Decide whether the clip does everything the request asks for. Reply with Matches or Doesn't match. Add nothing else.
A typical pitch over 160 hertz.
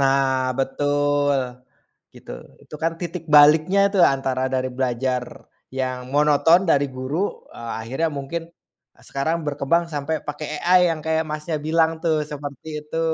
Doesn't match